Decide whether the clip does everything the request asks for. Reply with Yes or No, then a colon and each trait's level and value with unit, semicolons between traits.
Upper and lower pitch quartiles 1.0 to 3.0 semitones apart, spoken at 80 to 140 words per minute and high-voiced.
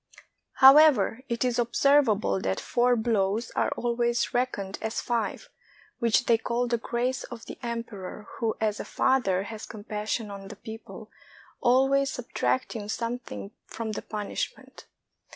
Yes: average, 2.7 semitones; slow, 135 wpm; high, 230 Hz